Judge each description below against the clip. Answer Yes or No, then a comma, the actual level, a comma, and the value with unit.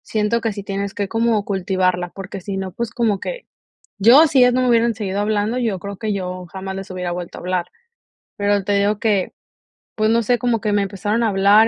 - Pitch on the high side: Yes, high, 205 Hz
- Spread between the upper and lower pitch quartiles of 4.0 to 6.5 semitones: No, average, 2.8 semitones